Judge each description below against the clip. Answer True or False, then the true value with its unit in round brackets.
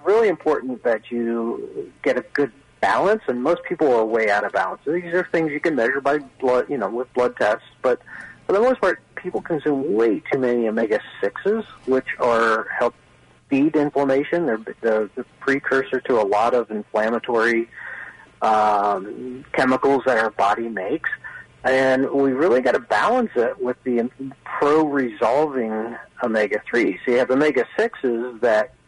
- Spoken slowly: False (165 wpm)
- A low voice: True (130 Hz)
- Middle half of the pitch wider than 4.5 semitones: False (4.1 semitones)